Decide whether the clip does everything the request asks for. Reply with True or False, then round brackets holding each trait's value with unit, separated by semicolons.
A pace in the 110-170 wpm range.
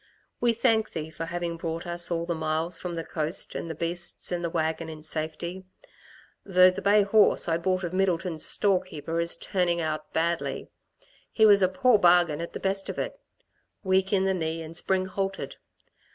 False (190 wpm)